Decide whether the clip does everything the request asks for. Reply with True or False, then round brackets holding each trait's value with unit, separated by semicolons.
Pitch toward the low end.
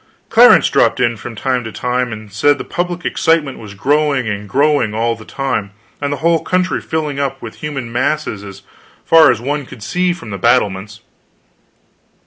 True (130 Hz)